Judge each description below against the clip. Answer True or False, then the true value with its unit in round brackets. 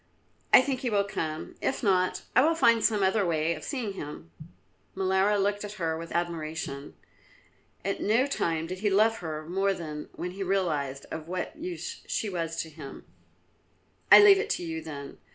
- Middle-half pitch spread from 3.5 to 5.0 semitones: True (4.7 semitones)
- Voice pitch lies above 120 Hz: True (185 Hz)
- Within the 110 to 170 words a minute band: False (185 wpm)